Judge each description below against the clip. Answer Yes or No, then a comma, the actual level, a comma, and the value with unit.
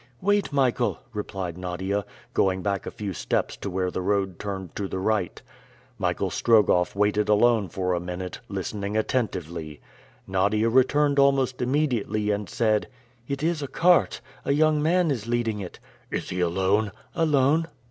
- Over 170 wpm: No, average, 155 wpm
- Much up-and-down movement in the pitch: Yes, wide, 5.7 semitones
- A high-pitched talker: No, low, 105 Hz